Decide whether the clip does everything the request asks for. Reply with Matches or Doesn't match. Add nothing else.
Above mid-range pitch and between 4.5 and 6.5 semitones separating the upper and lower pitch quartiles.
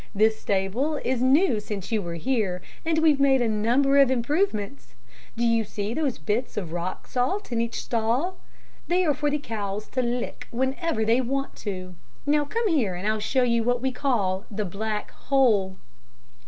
Matches